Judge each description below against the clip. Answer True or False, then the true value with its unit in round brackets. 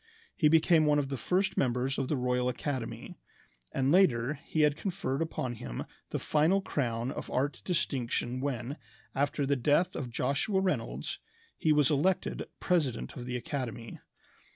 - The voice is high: False (140 Hz)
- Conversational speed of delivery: True (155 wpm)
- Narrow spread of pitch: False (3.8 semitones)